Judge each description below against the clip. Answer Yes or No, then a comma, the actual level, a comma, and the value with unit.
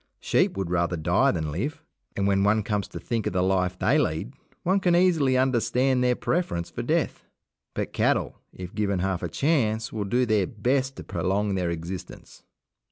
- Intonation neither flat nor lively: No, wide, 5.9 semitones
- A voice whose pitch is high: No, low, 105 Hz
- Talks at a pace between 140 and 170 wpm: No, average, 185 wpm